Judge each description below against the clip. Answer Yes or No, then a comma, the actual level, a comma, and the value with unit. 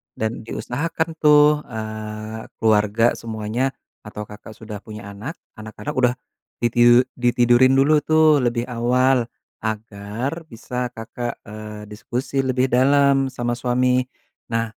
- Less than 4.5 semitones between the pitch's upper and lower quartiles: Yes, average, 3.1 semitones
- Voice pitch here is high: No, low, 120 Hz